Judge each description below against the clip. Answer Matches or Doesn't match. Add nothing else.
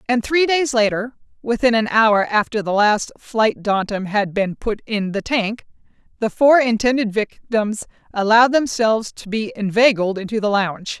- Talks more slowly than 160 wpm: Doesn't match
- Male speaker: Doesn't match